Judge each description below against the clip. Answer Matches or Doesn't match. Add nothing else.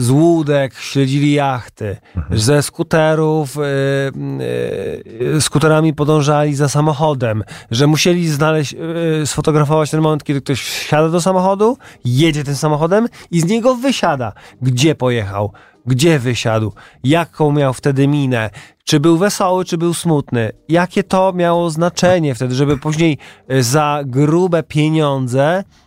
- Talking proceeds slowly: Doesn't match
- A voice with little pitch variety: Doesn't match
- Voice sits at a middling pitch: Matches